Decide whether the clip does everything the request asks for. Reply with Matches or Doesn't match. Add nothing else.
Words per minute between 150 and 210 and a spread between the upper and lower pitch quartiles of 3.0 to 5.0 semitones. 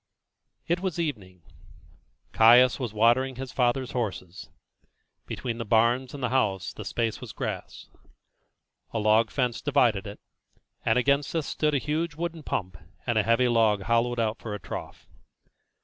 Matches